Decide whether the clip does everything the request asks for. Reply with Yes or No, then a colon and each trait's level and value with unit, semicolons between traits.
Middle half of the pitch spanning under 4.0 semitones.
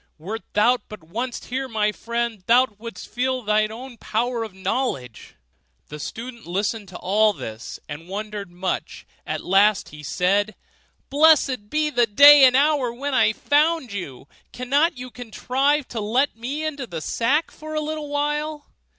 No: average, 5.2 semitones